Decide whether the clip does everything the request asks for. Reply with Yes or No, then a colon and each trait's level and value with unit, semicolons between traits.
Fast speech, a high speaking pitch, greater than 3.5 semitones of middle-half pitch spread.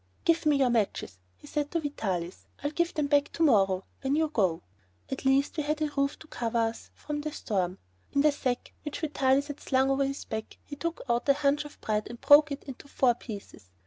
Yes: fast, 230 wpm; very high, 275 Hz; average, 4.3 semitones